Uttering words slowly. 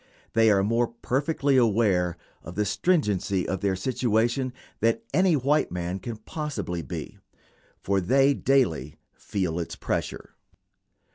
Yes: slow, 130 wpm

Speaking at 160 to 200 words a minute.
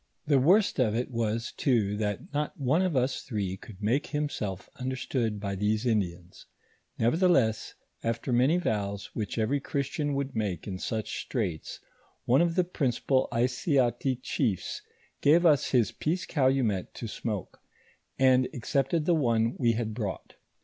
No: average, 150 wpm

